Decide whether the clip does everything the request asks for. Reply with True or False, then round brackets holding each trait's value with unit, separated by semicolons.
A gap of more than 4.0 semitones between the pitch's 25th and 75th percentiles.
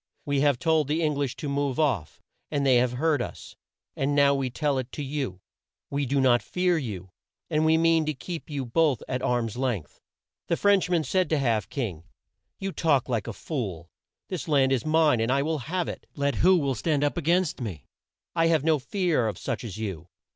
True (4.6 semitones)